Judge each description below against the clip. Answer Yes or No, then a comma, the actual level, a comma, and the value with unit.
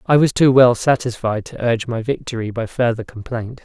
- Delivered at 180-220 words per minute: Yes, average, 200 wpm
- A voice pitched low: Yes, low, 120 Hz